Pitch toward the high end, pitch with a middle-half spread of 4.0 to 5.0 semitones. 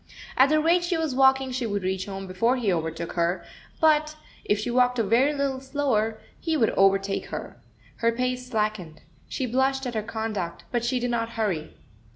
Yes: high, 235 Hz; average, 4.7 semitones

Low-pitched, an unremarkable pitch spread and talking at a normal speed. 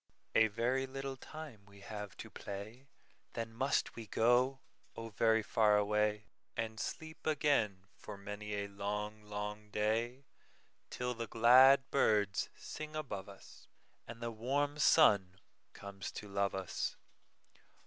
No: low, 110 Hz; average, 3.9 semitones; slow, 120 wpm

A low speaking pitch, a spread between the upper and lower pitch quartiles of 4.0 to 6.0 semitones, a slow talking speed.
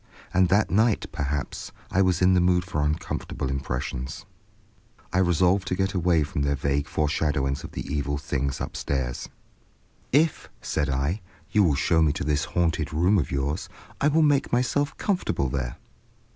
No: very low, 80 Hz; average, 5.1 semitones; average, 170 wpm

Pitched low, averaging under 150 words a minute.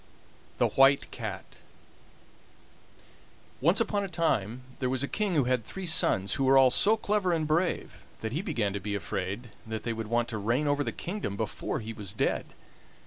No: low, 130 Hz; average, 190 wpm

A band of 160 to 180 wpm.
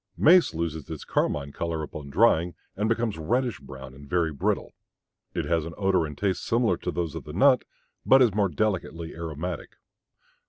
Yes: average, 175 wpm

